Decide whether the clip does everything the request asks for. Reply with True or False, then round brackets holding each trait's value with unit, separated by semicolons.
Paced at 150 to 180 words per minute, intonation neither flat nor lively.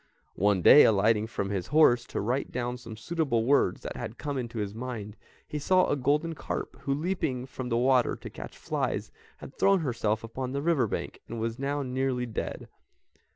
False (195 wpm; 3.9 semitones)